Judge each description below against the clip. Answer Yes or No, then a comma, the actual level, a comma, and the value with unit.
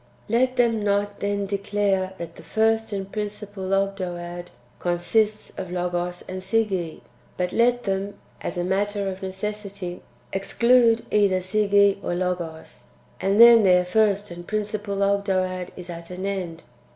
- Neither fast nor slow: Yes, average, 145 wpm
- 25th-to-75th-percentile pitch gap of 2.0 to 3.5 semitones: Yes, narrow, 2.5 semitones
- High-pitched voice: Yes, high, 195 Hz